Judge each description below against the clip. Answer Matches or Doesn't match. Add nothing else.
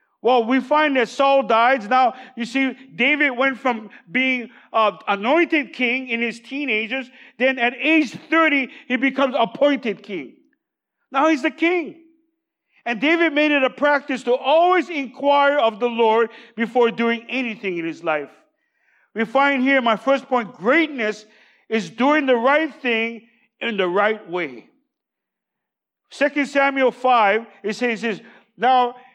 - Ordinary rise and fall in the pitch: Matches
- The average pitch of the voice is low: Doesn't match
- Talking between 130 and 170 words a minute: Matches